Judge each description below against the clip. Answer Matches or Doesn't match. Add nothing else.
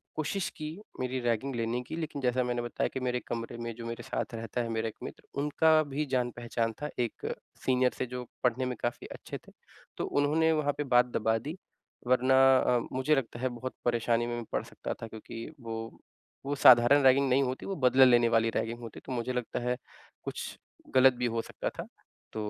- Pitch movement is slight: Matches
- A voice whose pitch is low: Matches